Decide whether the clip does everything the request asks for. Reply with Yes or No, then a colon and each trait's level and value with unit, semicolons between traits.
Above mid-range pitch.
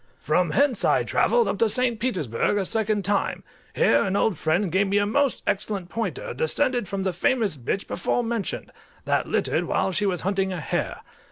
Yes: high, 205 Hz